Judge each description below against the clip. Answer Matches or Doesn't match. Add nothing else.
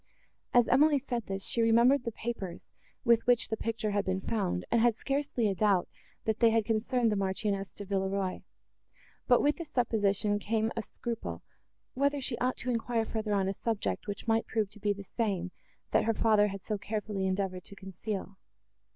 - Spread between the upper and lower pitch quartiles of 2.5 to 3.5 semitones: Matches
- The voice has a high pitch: Matches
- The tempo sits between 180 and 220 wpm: Matches